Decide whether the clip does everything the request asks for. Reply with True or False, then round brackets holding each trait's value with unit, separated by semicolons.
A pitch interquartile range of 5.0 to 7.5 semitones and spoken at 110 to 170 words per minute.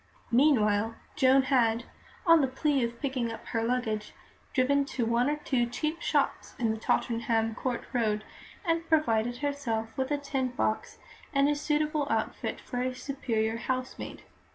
False (3.8 semitones; 155 wpm)